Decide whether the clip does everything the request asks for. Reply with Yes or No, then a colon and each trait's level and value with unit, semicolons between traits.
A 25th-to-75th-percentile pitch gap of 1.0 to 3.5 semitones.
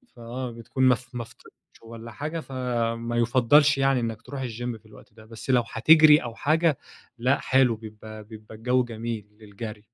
Yes: average, 2.7 semitones